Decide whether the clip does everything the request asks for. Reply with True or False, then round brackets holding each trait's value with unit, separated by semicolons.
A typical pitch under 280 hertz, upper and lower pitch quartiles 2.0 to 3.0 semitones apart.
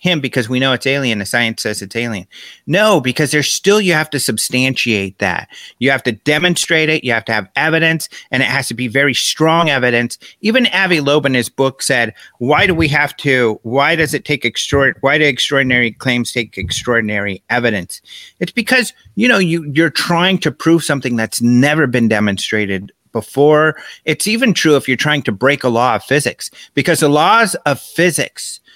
False (140 Hz; 4.9 semitones)